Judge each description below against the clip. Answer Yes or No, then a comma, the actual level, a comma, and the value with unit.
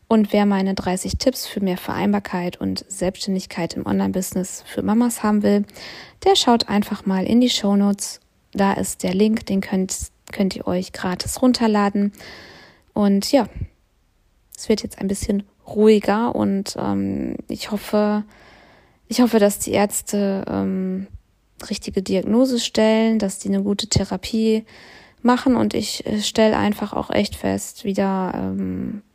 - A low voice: No, high, 205 Hz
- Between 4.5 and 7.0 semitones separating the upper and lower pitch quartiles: No, average, 2.9 semitones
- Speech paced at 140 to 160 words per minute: Yes, average, 145 wpm